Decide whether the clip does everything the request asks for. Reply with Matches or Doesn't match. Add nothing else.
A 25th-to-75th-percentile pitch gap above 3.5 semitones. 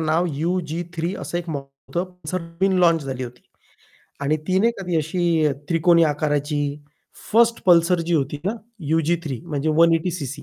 Doesn't match